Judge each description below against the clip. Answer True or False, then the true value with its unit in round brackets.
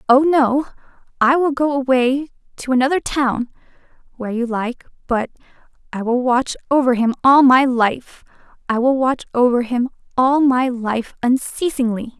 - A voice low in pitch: False (255 Hz)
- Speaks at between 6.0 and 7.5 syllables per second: False (4.6 syllables/s)